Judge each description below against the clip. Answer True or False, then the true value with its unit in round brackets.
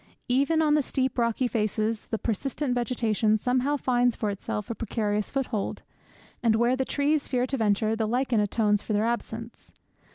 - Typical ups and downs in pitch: True (3.1 semitones)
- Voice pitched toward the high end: True (235 Hz)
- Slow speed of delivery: False (170 wpm)